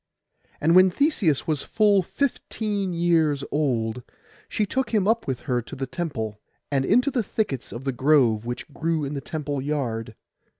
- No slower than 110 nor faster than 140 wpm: No, average, 170 wpm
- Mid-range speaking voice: Yes, medium, 150 Hz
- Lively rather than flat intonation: Yes, wide, 6.7 semitones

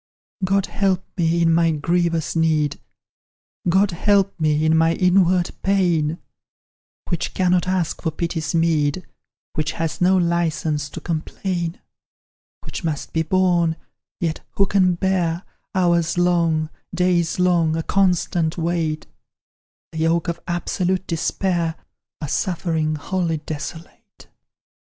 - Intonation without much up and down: Yes, narrow, 2.1 semitones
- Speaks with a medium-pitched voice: Yes, medium, 170 Hz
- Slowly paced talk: Yes, slow, 120 wpm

